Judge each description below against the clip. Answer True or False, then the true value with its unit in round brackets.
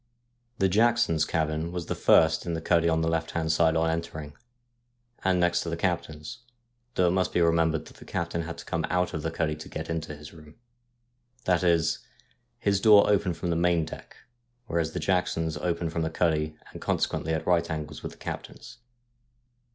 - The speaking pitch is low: True (85 Hz)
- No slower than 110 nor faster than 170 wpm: False (200 wpm)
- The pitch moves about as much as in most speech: False (1.6 semitones)